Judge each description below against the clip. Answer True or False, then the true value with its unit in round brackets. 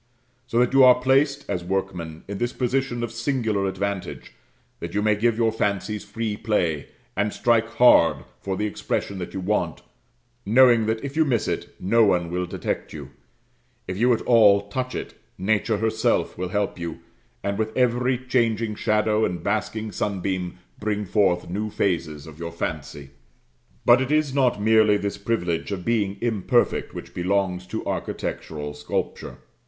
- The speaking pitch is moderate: False (105 Hz)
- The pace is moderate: True (165 wpm)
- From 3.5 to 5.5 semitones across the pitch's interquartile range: True (4.0 semitones)